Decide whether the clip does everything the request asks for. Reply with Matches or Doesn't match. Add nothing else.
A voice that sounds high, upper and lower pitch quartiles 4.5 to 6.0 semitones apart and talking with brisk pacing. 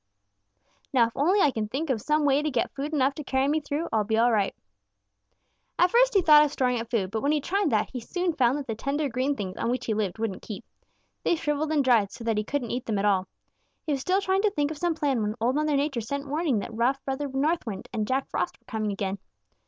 Matches